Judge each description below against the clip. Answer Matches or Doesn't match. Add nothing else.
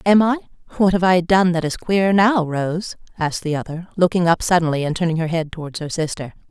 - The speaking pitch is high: Doesn't match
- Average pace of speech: Doesn't match